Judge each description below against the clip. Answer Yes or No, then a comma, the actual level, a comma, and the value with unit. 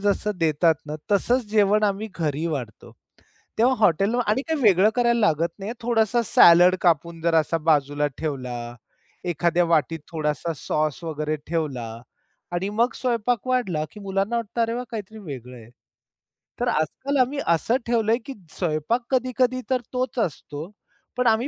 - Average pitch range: No, wide, 7.0 semitones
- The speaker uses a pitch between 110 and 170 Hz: No, medium, 185 Hz